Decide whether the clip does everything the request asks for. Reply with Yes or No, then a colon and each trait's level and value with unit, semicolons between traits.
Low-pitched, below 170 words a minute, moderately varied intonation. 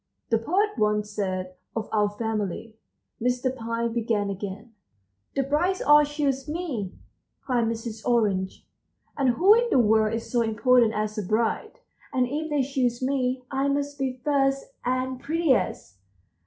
No: high, 245 Hz; average, 150 wpm; average, 4.2 semitones